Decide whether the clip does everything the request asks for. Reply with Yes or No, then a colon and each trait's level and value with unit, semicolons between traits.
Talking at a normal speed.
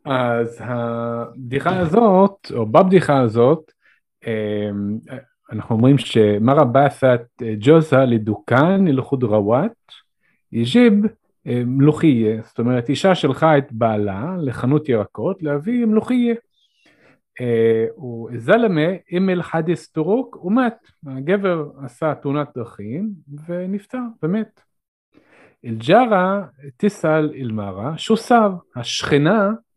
No: slow, 95 wpm